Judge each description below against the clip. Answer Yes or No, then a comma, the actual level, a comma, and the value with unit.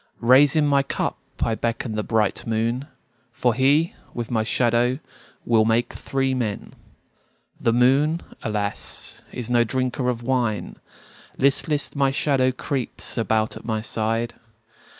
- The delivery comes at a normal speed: No, slow, 130 wpm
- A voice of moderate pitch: No, low, 120 Hz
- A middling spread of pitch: Yes, average, 3.0 semitones